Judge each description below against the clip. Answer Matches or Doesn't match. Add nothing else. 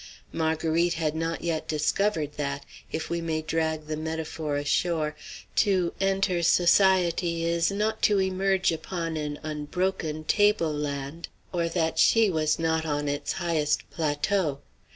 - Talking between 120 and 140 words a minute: Matches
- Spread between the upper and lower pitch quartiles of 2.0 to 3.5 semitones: Matches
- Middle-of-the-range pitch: Matches